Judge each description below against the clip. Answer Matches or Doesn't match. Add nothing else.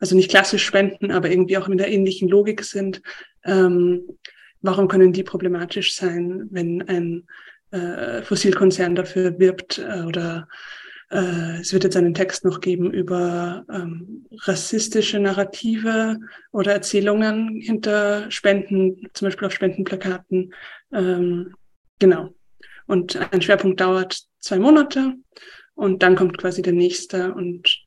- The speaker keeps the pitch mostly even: Matches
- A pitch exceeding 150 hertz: Matches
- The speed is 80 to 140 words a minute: Matches